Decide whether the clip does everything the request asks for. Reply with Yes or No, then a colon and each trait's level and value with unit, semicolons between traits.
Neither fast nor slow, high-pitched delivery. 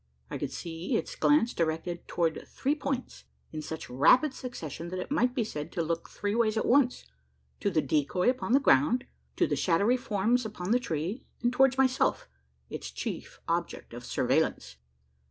Yes: average, 175 wpm; high, 210 Hz